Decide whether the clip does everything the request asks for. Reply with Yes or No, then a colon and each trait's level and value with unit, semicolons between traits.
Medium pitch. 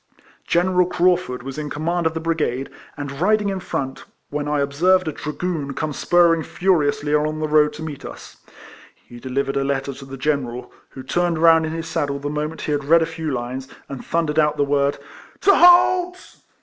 Yes: medium, 150 Hz